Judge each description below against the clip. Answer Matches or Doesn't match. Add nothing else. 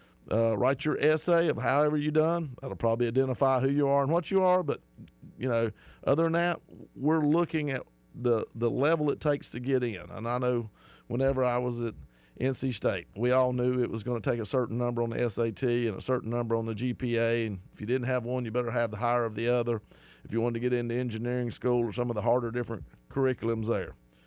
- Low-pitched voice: Matches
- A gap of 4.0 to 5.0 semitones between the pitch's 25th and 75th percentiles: Doesn't match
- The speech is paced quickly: Matches